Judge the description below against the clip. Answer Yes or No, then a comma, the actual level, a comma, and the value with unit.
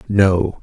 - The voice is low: Yes, low, 100 Hz